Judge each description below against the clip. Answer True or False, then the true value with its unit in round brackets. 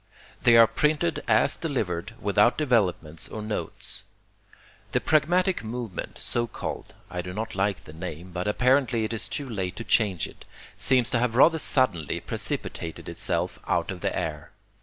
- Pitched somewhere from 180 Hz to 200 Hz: False (110 Hz)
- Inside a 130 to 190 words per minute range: True (160 wpm)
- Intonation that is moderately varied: False (5.7 semitones)